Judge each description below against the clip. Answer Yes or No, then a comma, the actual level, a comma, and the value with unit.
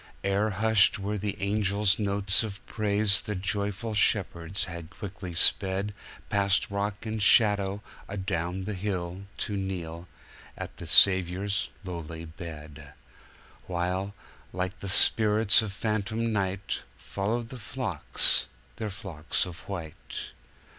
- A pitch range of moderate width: No, narrow, 2.3 semitones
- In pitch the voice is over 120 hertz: No, low, 100 Hz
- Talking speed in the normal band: No, slow, 120 wpm